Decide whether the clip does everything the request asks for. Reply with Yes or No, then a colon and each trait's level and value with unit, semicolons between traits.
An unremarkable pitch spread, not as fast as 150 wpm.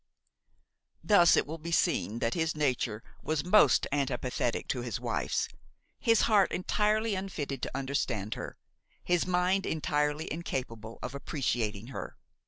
No: wide, 6.4 semitones; slow, 135 wpm